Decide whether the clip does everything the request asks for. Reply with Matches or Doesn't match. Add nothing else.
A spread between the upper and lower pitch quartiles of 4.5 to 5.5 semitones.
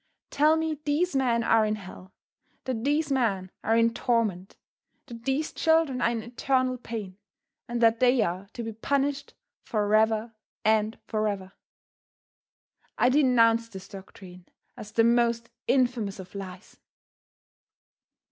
Doesn't match